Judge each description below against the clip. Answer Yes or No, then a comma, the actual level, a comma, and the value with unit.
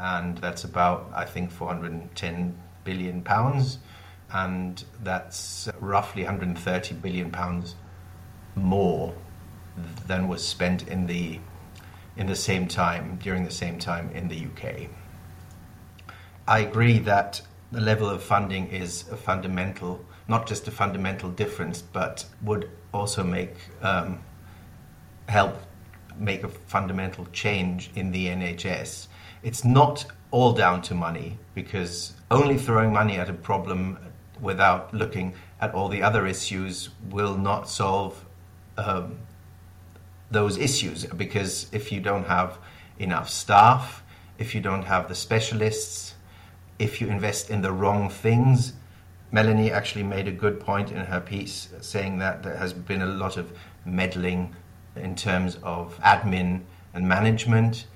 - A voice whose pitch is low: Yes, very low, 95 Hz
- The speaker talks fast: No, average, 140 wpm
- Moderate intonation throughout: No, narrow, 2.1 semitones